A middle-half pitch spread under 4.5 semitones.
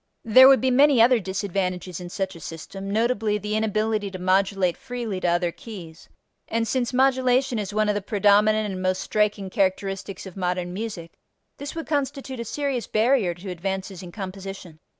Yes: average, 3.8 semitones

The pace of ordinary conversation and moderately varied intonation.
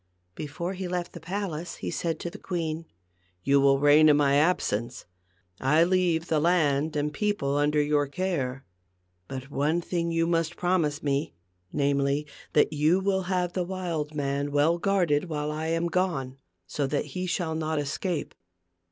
Yes: average, 165 wpm; average, 3.4 semitones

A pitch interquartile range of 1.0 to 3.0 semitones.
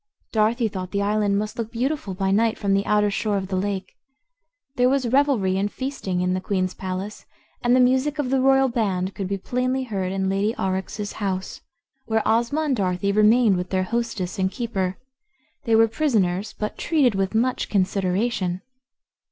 No: average, 3.9 semitones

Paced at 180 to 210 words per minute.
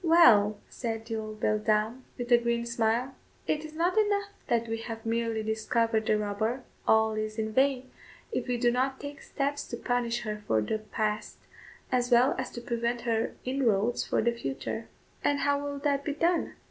Yes: average, 185 wpm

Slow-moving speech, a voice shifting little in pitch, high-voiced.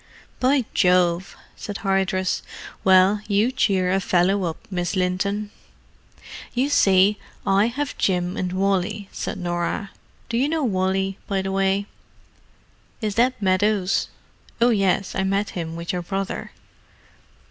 Yes: slow, 130 wpm; narrow, 2.1 semitones; high, 195 Hz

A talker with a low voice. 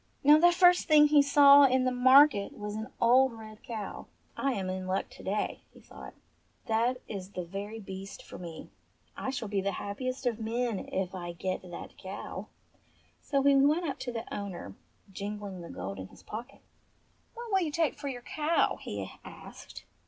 No: high, 225 Hz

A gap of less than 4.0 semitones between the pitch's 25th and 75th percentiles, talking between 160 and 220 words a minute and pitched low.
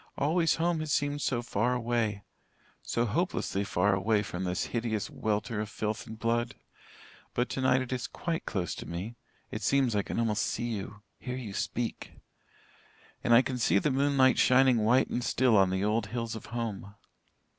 Yes: average, 3.5 semitones; average, 190 wpm; low, 115 Hz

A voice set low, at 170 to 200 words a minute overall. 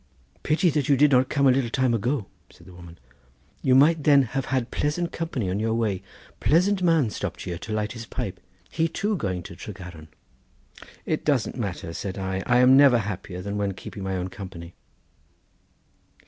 Yes: low, 115 Hz; average, 190 wpm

